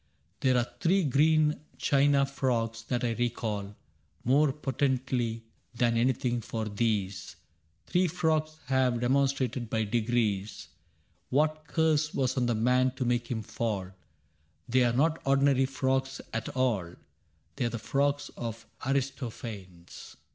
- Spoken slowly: Yes, slow, 130 wpm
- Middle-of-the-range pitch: No, low, 125 Hz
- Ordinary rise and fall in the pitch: Yes, average, 3.3 semitones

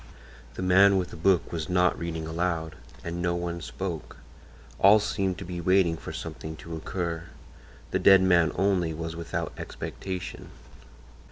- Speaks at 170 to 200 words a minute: No, average, 155 wpm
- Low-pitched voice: Yes, very low, 85 Hz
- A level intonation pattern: Yes, narrow, 2.1 semitones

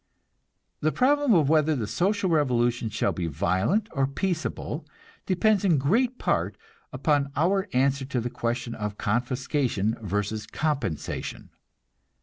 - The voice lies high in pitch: No, low, 135 Hz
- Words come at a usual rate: No, slow, 130 wpm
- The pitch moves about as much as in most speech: No, wide, 7.1 semitones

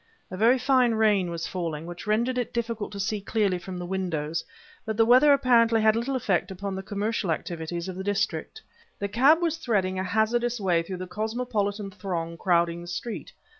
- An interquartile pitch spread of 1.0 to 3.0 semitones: No, average, 4.3 semitones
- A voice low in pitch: No, high, 205 Hz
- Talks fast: No, average, 195 wpm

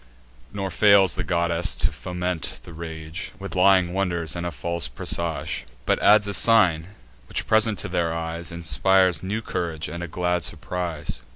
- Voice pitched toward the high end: No, very low, 85 Hz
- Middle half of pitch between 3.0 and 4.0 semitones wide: No, narrow, 2.5 semitones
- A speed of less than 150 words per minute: No, average, 165 wpm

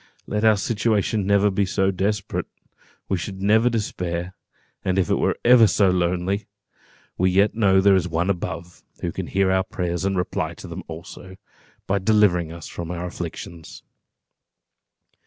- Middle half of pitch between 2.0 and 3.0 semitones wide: Yes, narrow, 2.5 semitones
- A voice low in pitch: Yes, very low, 95 Hz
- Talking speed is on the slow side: No, average, 165 wpm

